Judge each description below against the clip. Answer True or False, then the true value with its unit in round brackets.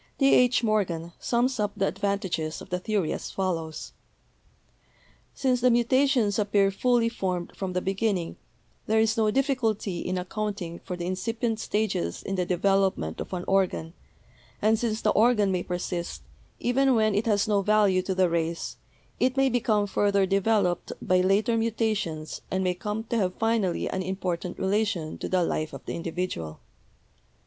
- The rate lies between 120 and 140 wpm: False (170 wpm)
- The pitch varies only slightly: False (3.6 semitones)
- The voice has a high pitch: True (200 Hz)